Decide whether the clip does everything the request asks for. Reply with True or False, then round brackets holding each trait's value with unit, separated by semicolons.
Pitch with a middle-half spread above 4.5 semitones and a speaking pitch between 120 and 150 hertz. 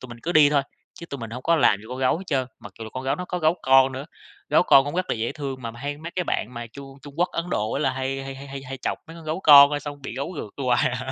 False (3.0 semitones; 135 Hz)